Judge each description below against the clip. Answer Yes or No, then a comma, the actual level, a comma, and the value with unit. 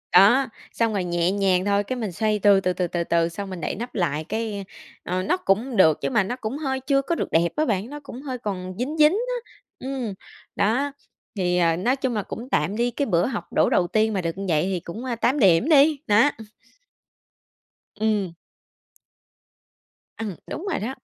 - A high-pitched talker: Yes, high, 210 Hz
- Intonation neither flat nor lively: No, wide, 5.9 semitones